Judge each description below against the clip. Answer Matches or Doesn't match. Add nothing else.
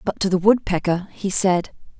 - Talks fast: Doesn't match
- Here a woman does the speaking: Matches